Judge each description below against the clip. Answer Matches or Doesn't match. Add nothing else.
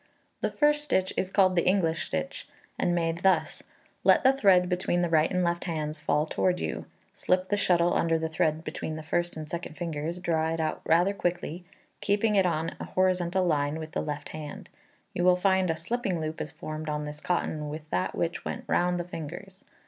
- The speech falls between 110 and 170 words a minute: Doesn't match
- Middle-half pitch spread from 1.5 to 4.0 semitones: Matches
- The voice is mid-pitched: Matches